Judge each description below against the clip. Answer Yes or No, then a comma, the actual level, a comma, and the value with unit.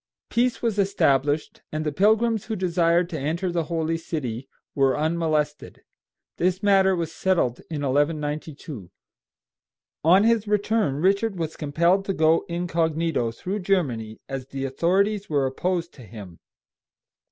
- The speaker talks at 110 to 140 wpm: Yes, slow, 135 wpm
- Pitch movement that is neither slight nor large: Yes, average, 4.8 semitones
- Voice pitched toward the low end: No, medium, 165 Hz